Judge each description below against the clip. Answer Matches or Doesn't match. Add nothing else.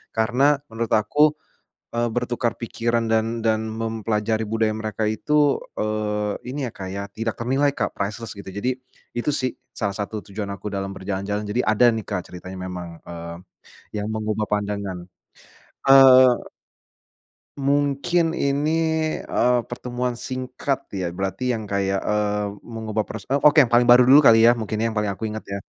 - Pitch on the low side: Matches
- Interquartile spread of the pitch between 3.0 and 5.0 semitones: Matches